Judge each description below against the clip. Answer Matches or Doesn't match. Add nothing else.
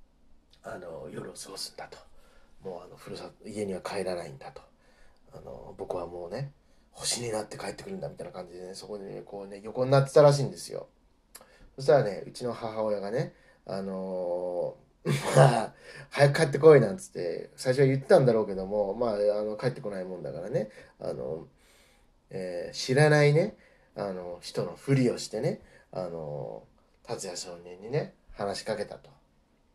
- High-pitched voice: Doesn't match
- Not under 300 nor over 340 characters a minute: Matches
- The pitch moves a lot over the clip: Matches